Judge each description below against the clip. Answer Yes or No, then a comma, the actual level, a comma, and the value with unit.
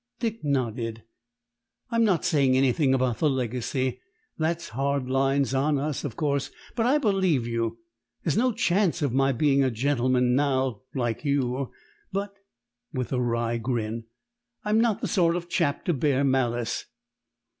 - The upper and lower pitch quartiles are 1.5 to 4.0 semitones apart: No, average, 4.6 semitones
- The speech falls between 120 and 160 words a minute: Yes, average, 155 wpm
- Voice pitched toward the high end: No, low, 135 Hz